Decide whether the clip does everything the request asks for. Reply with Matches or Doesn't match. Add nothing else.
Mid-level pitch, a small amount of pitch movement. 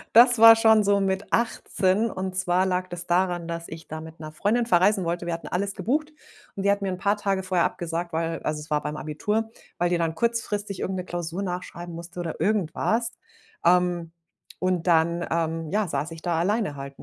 Doesn't match